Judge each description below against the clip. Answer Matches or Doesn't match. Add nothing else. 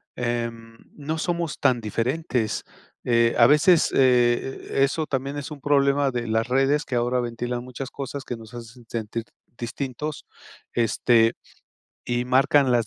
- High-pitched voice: Doesn't match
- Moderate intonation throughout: Matches